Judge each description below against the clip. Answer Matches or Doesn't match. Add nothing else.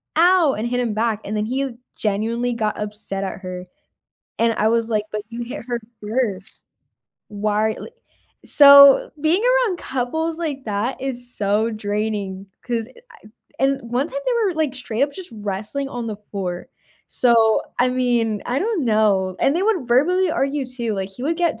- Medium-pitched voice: Doesn't match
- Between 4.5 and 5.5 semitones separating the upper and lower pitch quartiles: Matches